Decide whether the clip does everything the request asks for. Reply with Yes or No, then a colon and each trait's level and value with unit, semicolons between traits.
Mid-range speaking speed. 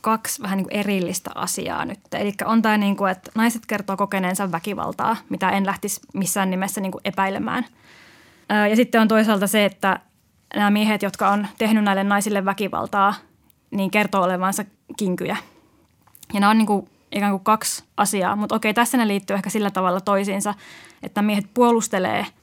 No: fast, 170 wpm